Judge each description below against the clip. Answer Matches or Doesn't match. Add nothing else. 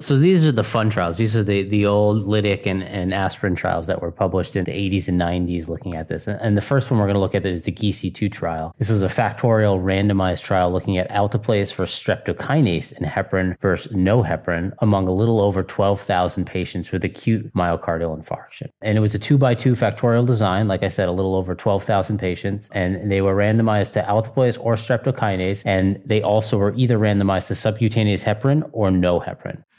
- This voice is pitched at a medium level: Doesn't match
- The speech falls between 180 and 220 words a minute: Matches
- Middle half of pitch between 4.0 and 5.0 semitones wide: Doesn't match